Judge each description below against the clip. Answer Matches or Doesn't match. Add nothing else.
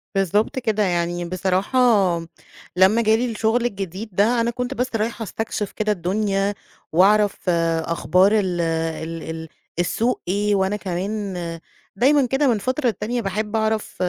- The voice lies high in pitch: Matches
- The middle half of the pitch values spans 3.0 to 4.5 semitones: Matches